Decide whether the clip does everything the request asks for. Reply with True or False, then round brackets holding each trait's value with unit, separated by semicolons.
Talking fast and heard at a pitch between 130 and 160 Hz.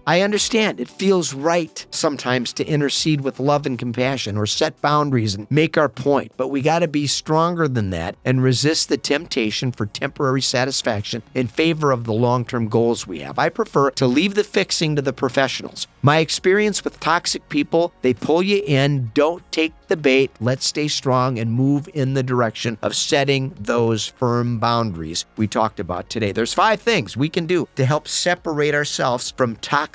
False (185 wpm; 135 Hz)